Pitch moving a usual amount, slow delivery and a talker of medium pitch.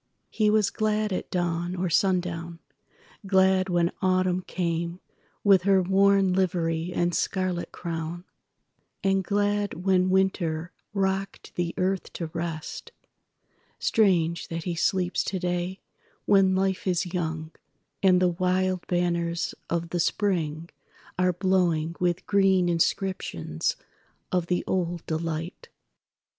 No: narrow, 2.0 semitones; slow, 105 wpm; medium, 180 Hz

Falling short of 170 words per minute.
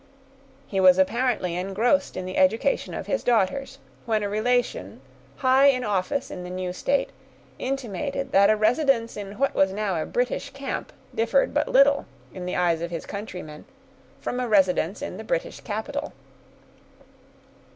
Yes: average, 160 wpm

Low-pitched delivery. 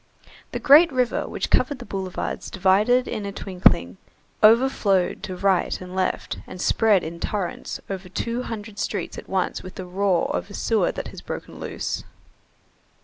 No: high, 195 Hz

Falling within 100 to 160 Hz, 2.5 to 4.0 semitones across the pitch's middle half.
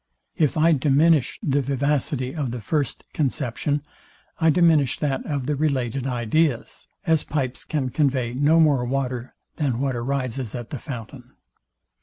Yes: low, 135 Hz; average, 3.1 semitones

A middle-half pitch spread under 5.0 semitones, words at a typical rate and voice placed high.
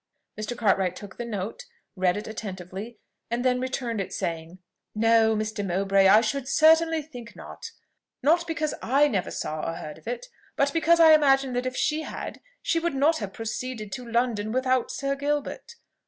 No: wide, 5.5 semitones; average, 180 wpm; high, 240 Hz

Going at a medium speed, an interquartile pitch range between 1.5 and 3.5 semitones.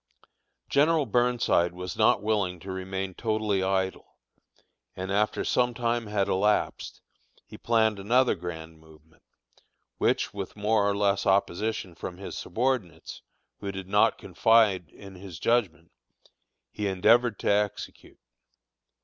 No: slow, 125 wpm; average, 3.1 semitones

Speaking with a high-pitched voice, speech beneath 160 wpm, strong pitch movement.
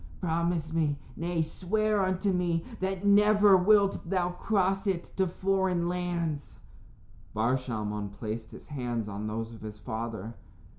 No: medium, 170 Hz; average, 140 wpm; wide, 8.3 semitones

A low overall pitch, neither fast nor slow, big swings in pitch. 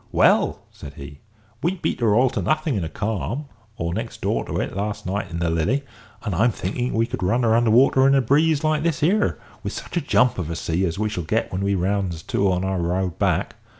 No: low, 105 Hz; fast, 245 wpm; wide, 6.8 semitones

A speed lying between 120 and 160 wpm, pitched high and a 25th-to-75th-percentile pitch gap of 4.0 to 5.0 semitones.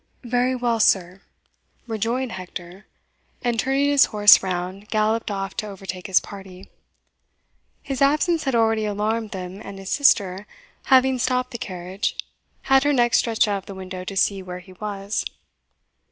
Yes: average, 155 wpm; high, 210 Hz; average, 4.3 semitones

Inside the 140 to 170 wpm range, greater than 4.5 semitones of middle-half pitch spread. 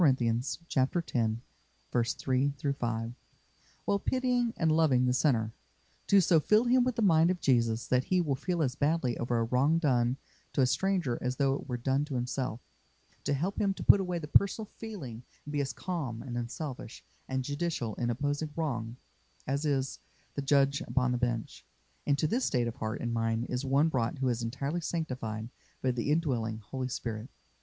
No: average, 180 wpm; average, 4.9 semitones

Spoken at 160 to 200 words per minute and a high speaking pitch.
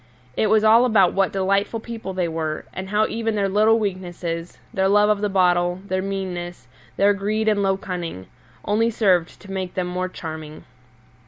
Yes: average, 180 wpm; high, 195 Hz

